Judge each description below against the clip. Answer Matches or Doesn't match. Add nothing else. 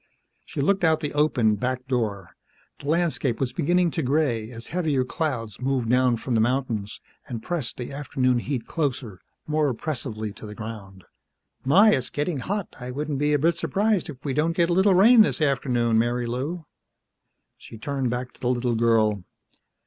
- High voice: Doesn't match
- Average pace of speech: Matches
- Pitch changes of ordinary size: Matches